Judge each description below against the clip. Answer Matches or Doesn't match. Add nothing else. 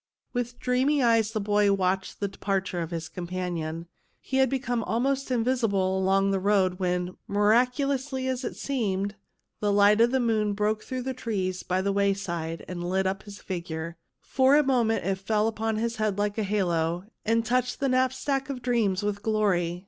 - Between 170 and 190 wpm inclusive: Matches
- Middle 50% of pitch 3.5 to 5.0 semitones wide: Matches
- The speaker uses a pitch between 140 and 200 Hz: Doesn't match